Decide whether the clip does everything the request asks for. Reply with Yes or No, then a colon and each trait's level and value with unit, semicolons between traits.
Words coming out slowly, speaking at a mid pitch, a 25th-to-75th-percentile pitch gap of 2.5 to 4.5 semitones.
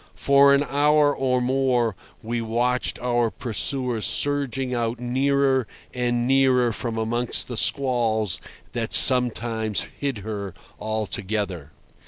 No: slow, 115 wpm; low, 120 Hz; average, 3.0 semitones